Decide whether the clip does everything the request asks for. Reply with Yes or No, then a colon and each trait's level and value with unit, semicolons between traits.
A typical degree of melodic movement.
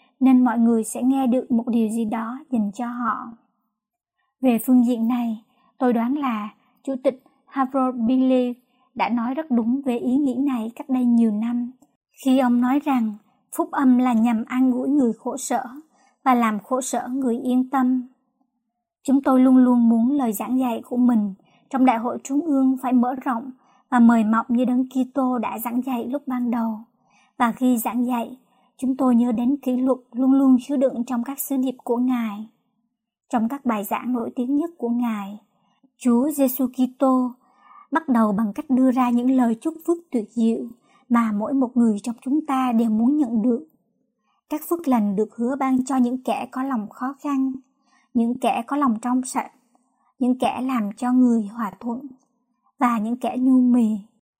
No: narrow, 1.8 semitones